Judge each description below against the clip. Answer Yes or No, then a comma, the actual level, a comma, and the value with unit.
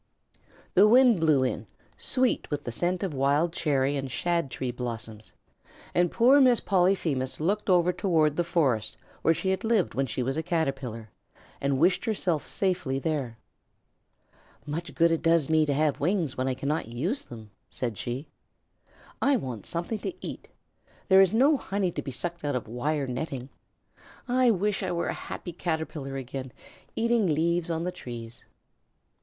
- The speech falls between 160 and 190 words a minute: Yes, average, 170 wpm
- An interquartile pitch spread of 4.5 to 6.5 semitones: Yes, wide, 5.6 semitones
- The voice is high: No, medium, 160 Hz